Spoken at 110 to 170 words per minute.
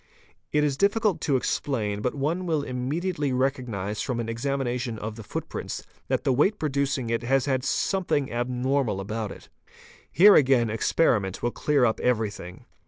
Yes: average, 160 wpm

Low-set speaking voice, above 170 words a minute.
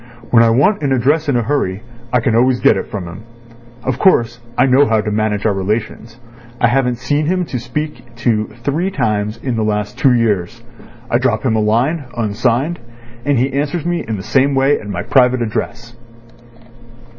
Yes: low, 120 Hz; average, 195 wpm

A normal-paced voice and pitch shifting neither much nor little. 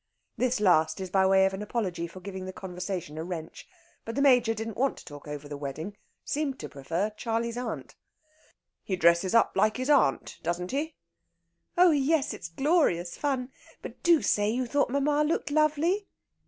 No: average, 180 wpm; wide, 7.7 semitones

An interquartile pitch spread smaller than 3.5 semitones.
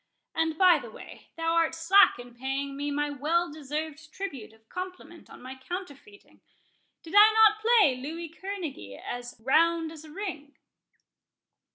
No: average, 4.6 semitones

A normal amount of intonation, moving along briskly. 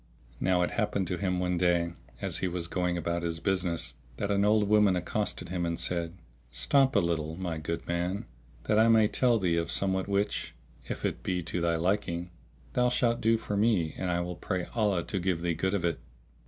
Yes: average, 3.0 semitones; fast, 210 wpm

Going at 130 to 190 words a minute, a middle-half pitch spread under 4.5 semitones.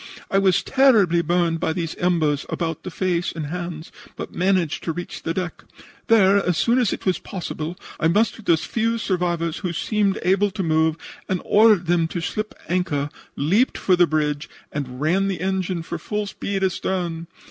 Yes: average, 180 wpm; average, 3.0 semitones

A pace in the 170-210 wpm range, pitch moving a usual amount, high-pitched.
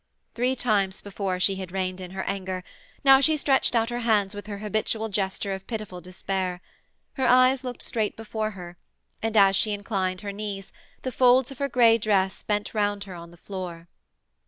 Yes: average, 190 wpm; average, 3.2 semitones; high, 205 Hz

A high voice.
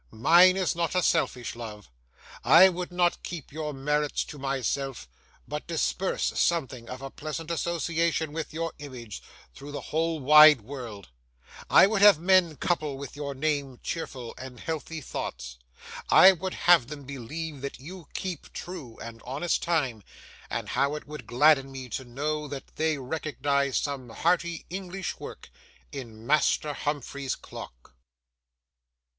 No: medium, 150 Hz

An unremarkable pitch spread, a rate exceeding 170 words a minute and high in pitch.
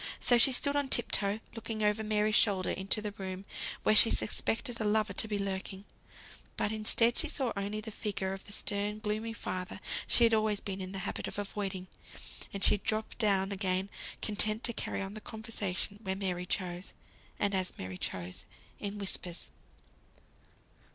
No: narrow, 2.2 semitones; average, 180 wpm; high, 205 Hz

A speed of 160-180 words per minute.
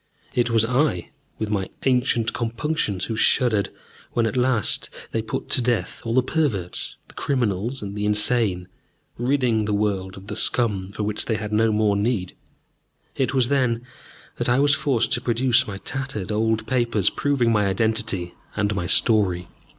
Yes: average, 170 wpm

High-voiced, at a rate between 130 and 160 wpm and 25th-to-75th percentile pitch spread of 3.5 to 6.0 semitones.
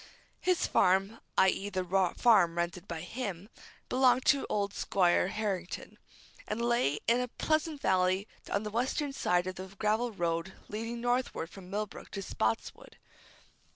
Yes: high, 200 Hz; average, 145 wpm; average, 4.6 semitones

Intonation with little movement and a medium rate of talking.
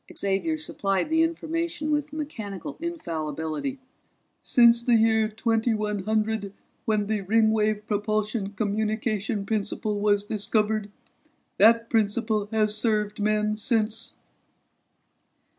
No: narrow, 1.9 semitones; slow, 95 wpm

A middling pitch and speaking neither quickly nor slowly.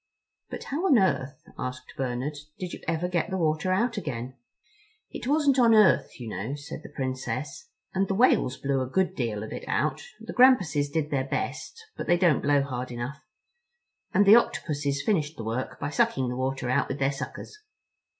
Yes: medium, 145 Hz; average, 190 wpm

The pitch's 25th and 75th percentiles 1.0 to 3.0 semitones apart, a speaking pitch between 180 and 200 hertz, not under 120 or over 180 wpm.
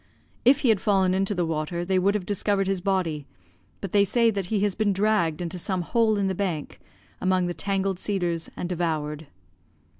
No: average, 2.7 semitones; high, 190 Hz; average, 200 wpm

